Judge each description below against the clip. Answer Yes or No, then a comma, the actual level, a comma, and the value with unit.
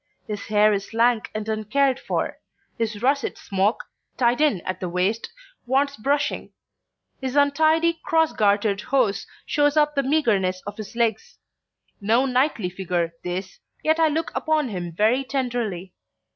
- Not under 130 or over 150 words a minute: Yes, average, 145 wpm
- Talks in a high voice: Yes, high, 235 Hz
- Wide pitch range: Yes, wide, 5.8 semitones